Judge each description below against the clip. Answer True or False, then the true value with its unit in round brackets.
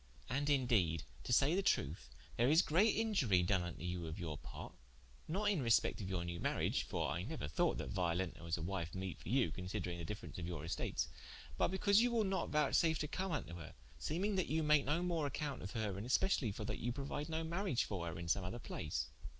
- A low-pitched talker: True (115 Hz)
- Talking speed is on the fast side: True (230 wpm)